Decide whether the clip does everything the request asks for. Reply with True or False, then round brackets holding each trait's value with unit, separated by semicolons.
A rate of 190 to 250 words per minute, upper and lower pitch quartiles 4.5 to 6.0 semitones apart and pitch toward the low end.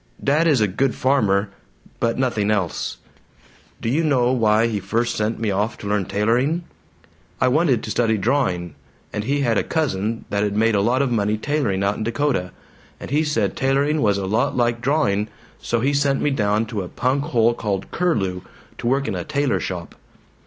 True (195 wpm; 5.0 semitones; 115 Hz)